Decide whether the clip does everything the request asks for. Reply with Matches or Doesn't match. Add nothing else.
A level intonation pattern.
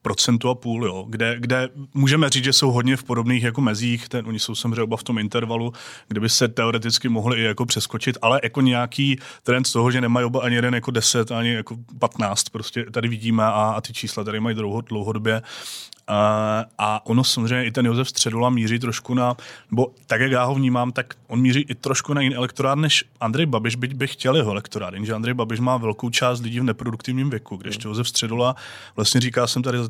Matches